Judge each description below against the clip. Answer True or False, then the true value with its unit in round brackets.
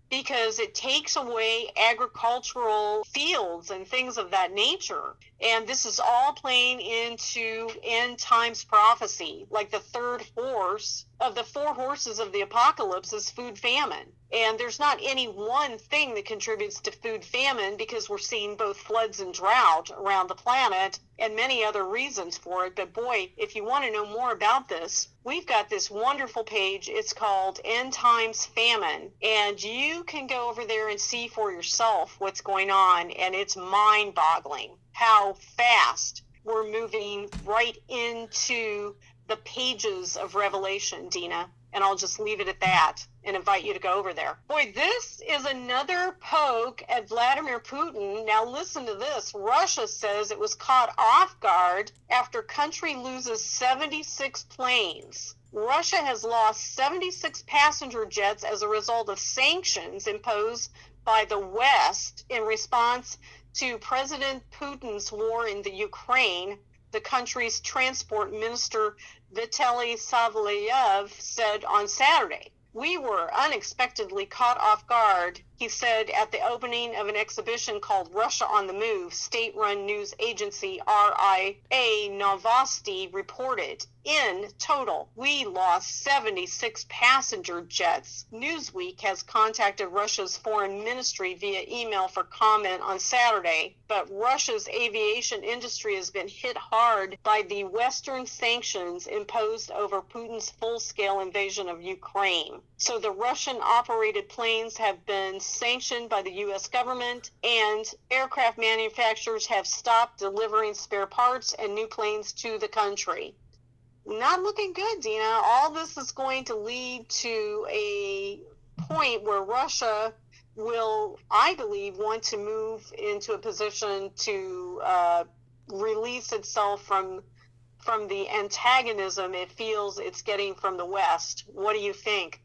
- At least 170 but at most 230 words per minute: False (145 wpm)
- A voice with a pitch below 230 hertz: False (240 Hz)